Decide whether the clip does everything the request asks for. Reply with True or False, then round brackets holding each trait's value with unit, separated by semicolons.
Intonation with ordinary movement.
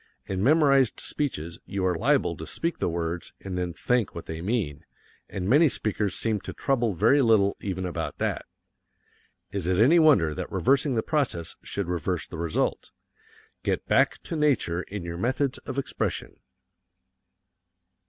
False (7.3 semitones)